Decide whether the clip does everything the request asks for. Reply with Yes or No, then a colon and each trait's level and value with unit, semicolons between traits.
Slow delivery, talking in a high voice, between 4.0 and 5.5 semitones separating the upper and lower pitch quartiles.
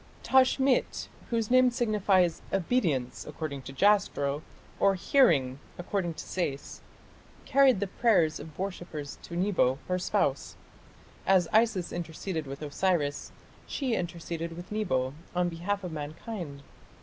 No: slow, 125 wpm; medium, 175 Hz; average, 5.2 semitones